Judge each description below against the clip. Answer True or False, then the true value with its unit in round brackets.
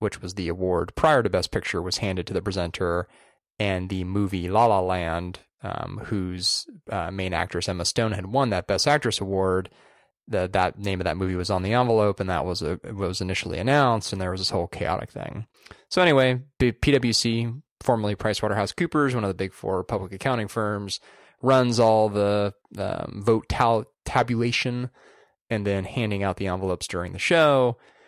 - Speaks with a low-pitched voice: True (100 Hz)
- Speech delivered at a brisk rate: False (185 wpm)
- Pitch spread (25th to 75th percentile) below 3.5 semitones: False (4.0 semitones)